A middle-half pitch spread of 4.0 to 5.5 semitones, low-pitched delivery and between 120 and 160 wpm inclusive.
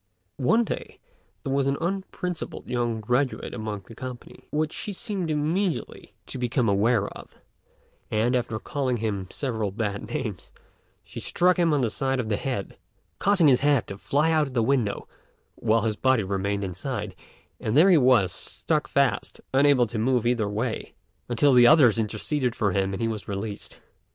No: average, 5.0 semitones; low, 125 Hz; average, 175 wpm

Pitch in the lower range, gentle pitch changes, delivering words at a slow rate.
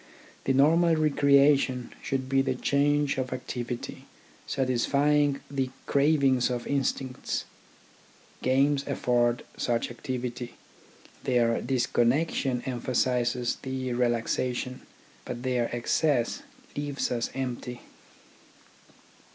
Yes: low, 130 Hz; narrow, 2.3 semitones; slow, 90 wpm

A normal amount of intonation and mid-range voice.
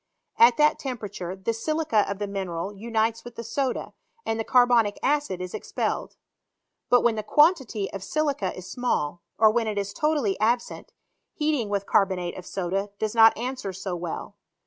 No: average, 4.0 semitones; high, 220 Hz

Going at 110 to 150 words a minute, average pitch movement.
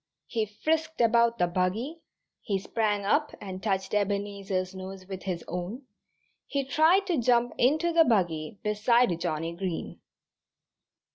Yes: slow, 135 wpm; average, 4.9 semitones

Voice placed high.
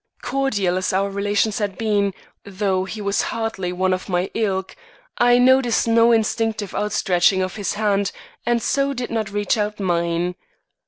Yes: high, 205 Hz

